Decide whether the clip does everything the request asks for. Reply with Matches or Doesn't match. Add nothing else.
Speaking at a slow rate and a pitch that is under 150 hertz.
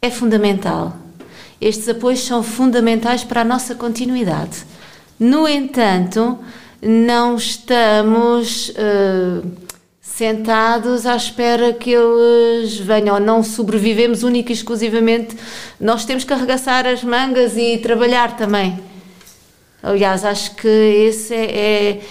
Doesn't match